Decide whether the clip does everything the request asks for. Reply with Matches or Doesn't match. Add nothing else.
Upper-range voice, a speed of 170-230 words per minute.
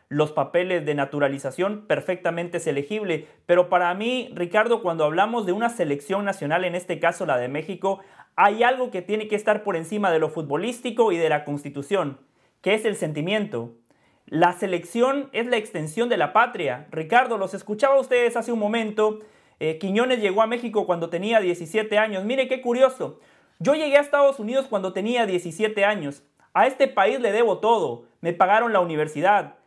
Matches